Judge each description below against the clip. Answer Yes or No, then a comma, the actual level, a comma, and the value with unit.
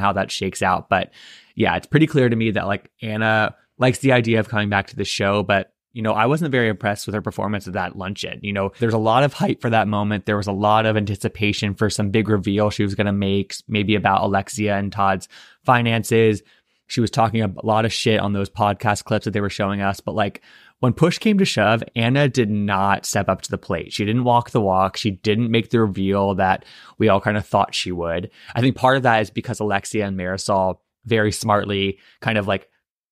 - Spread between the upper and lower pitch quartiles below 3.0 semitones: Yes, narrow, 2.4 semitones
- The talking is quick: Yes, fast, 235 wpm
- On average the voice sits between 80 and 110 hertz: Yes, low, 105 Hz